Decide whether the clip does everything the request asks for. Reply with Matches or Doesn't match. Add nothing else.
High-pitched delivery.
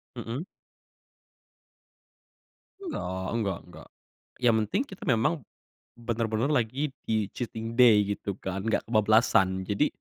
Doesn't match